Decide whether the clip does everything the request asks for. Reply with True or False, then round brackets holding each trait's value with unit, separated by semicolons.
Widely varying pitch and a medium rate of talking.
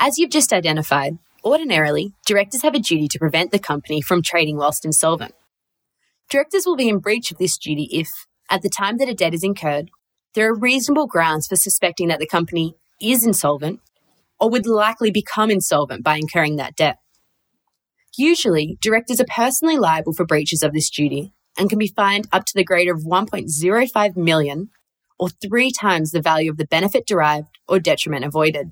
True (5.7 semitones; 180 wpm)